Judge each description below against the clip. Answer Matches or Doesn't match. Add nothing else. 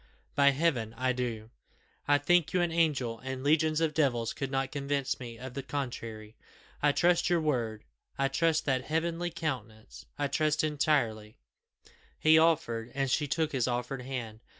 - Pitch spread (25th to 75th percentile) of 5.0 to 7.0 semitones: Doesn't match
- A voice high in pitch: Doesn't match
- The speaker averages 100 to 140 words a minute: Doesn't match